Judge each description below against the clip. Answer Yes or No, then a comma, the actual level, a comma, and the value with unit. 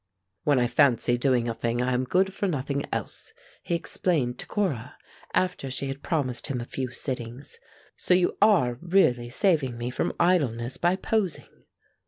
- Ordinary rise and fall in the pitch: No, wide, 6.3 semitones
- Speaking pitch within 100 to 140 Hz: Yes, low, 135 Hz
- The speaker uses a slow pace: No, average, 170 wpm